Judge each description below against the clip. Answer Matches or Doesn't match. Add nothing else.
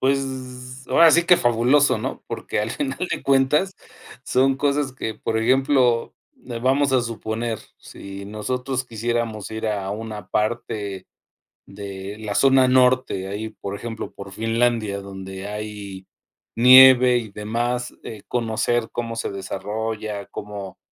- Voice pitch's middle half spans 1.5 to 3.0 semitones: Doesn't match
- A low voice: Matches